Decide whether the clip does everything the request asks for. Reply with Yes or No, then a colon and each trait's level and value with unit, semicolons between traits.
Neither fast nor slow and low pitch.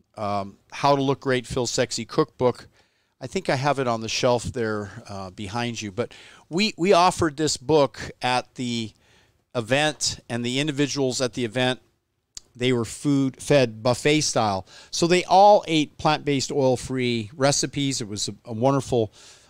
Yes: average, 165 wpm; low, 125 Hz